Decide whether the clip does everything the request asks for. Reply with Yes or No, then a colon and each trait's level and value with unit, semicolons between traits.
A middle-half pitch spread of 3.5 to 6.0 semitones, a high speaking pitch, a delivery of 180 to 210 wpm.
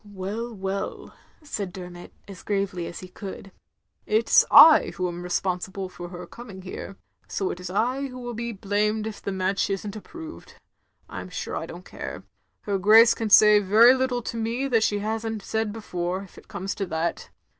No: average, 3.1 semitones; high, 205 Hz; average, 195 wpm